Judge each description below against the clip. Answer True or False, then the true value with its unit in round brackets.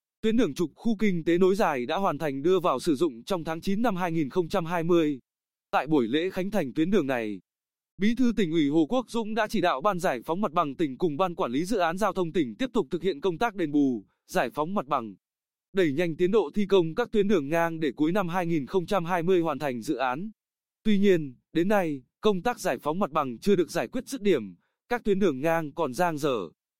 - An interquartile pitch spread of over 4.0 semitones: True (4.7 semitones)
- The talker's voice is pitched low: False (185 Hz)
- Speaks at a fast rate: False (235 wpm)